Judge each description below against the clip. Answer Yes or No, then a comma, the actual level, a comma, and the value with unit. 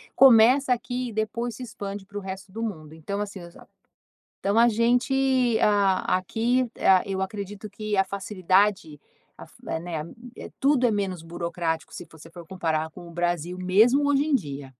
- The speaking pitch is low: No, high, 200 Hz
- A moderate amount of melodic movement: Yes, average, 4.9 semitones